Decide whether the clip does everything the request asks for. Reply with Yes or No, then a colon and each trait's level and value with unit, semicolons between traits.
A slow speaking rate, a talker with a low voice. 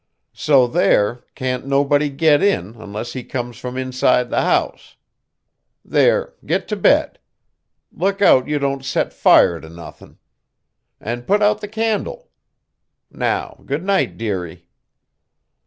Yes: slow, 130 wpm; low, 130 Hz